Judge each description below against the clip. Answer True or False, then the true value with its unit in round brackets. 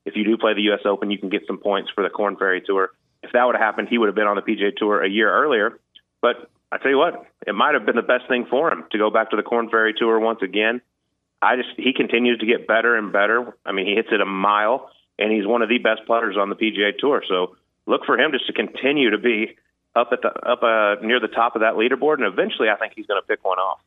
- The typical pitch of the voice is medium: False (110 Hz)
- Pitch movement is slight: True (2.2 semitones)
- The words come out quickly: True (285 wpm)